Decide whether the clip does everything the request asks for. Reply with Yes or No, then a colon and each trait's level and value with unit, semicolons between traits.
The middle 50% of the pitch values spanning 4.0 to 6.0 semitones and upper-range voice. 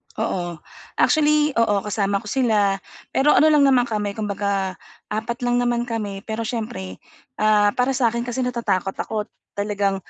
No: average, 3.4 semitones; high, 220 Hz